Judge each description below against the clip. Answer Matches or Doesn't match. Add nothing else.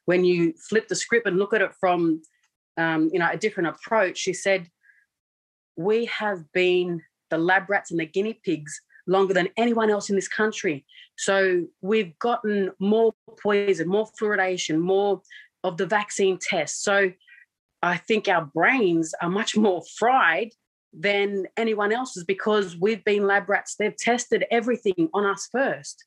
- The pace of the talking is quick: Doesn't match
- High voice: Matches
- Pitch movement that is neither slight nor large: Matches